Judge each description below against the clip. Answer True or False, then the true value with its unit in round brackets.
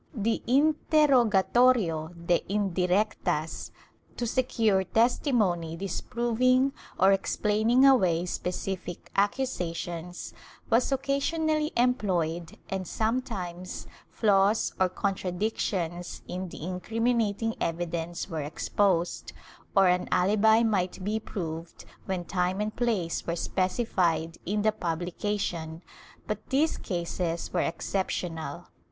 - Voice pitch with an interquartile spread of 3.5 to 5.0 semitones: True (4.5 semitones)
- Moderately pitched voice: False (195 Hz)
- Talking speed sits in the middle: False (100 wpm)